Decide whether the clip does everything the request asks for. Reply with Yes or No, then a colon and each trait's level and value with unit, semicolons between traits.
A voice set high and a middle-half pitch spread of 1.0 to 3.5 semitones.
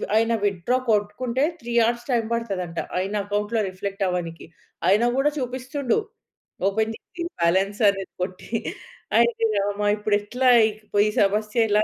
Yes: high, 210 Hz; average, 3.1 semitones